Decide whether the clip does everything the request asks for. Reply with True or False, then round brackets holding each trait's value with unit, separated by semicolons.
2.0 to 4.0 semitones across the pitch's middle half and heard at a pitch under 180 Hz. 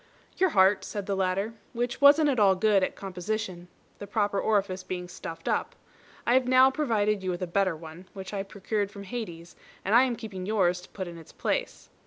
False (3.3 semitones; 200 Hz)